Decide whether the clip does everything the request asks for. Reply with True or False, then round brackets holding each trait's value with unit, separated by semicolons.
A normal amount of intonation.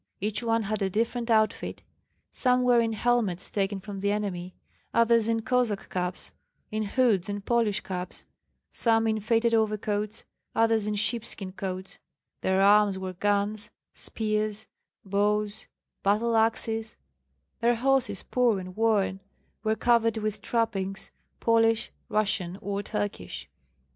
False (2.3 semitones)